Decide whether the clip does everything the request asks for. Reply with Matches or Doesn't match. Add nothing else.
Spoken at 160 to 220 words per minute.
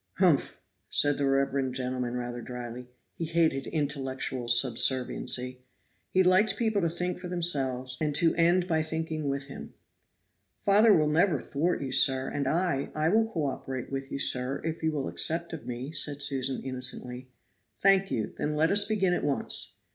Matches